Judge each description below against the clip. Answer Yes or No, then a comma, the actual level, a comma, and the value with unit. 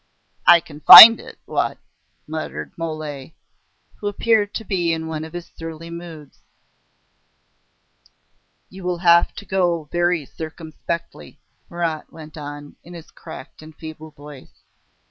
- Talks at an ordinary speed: No, slow, 130 wpm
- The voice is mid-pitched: Yes, medium, 165 Hz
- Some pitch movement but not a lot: No, narrow, 2.0 semitones